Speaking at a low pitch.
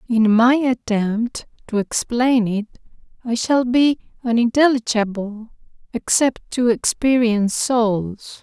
No: high, 235 Hz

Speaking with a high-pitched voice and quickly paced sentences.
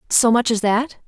Yes: high, 230 Hz; fast, 225 wpm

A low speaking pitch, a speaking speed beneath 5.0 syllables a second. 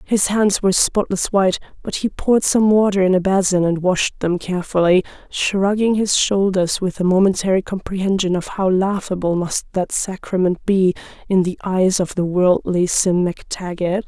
No: high, 190 Hz; 4.8 syllables/s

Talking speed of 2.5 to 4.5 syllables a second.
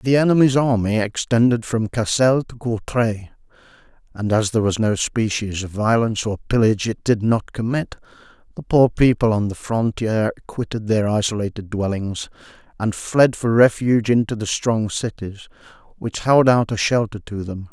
No: 4.9 syllables/s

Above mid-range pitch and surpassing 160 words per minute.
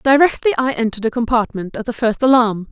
Yes: high, 240 Hz; average, 200 wpm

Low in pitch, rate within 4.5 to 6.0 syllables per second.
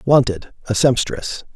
No: low, 120 Hz; 4.1 syllables/s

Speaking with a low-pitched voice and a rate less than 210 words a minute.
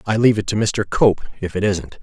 No: low, 105 Hz; fast, 265 wpm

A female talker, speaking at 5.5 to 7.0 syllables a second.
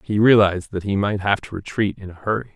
No: male; 6.3 syllables/s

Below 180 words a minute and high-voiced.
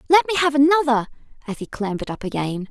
No: average, 200 wpm; very high, 260 Hz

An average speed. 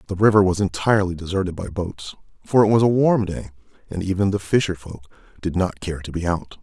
No: fast, 215 wpm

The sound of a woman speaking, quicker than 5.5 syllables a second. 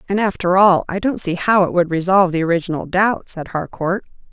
Yes: female; 5.8 syllables/s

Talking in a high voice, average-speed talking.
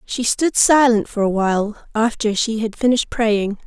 Yes: high, 225 Hz; average, 180 wpm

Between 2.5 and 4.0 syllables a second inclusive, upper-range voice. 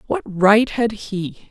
Yes: 3.0 syllables/s; high, 205 Hz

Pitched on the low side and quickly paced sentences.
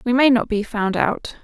No: high, 225 Hz; fast, 250 wpm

